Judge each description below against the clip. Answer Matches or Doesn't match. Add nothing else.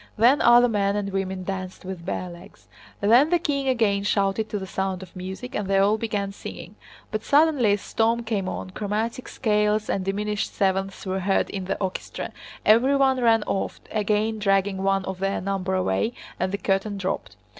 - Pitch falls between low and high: Doesn't match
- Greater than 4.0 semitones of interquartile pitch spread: Doesn't match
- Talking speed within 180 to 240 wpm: Matches